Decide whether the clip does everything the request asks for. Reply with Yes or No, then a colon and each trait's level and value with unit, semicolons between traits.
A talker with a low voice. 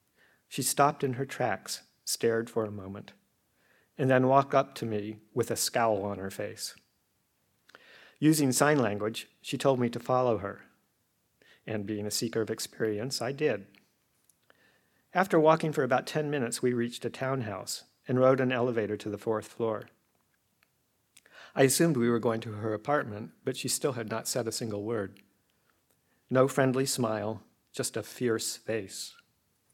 Yes: low, 120 Hz